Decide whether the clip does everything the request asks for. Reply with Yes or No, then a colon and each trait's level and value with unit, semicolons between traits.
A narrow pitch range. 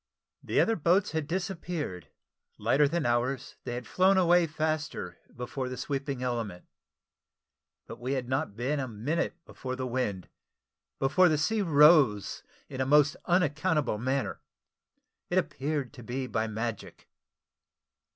No: average, 4.6 semitones